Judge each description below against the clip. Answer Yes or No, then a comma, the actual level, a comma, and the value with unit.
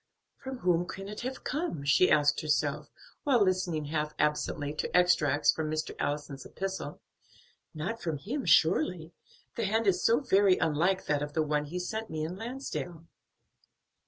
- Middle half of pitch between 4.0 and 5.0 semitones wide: Yes, average, 4.4 semitones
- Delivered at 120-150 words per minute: No, average, 160 wpm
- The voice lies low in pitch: No, medium, 170 Hz